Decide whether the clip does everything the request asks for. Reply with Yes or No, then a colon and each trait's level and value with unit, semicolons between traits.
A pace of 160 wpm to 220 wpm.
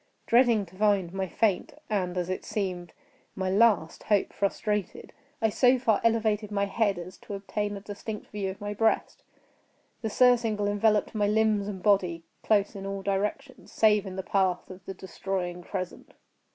Yes: average, 165 wpm